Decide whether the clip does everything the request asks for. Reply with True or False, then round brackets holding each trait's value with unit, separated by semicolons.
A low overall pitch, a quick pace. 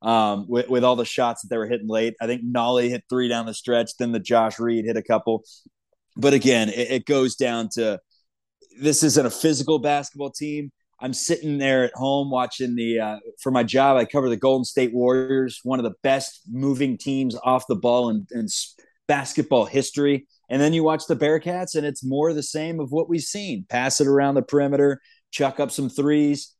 True (130 Hz; 210 wpm)